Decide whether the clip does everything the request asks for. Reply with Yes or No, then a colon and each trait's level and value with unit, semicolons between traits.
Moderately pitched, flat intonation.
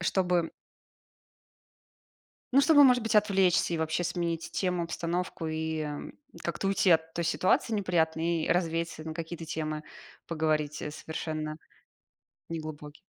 Yes: medium, 165 Hz; narrow, 2.2 semitones